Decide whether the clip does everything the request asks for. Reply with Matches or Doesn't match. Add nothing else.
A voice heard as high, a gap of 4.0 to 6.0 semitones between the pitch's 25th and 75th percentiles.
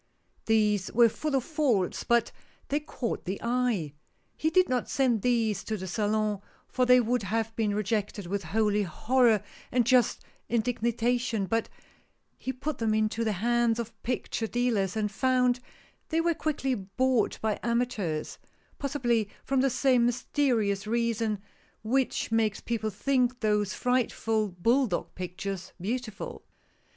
Doesn't match